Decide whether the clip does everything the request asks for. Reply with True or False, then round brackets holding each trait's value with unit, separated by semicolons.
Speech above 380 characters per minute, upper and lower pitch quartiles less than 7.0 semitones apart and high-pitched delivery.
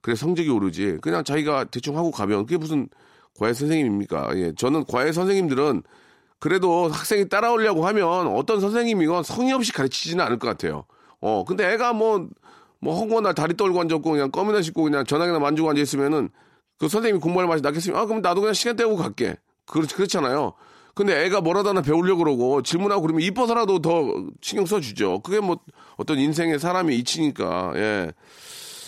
False (420 characters per minute; 5.3 semitones; 175 Hz)